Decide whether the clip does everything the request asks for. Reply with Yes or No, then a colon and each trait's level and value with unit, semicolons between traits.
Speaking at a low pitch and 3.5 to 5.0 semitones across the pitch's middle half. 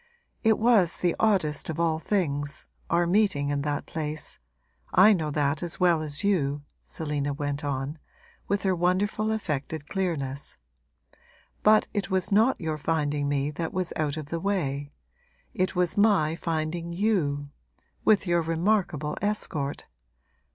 No: medium, 165 Hz; average, 4.6 semitones